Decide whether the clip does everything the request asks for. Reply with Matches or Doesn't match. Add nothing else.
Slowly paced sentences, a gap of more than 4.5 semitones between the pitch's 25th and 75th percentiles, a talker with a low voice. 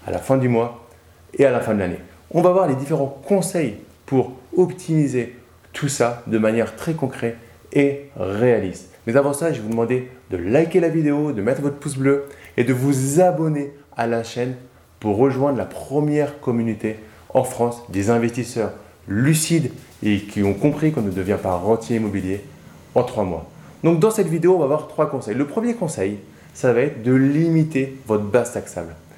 Doesn't match